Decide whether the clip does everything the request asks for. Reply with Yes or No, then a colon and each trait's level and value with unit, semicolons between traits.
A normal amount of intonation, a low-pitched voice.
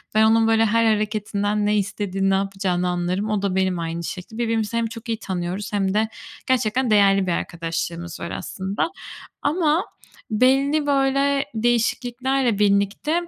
No: average, 3.7 semitones; high, 210 Hz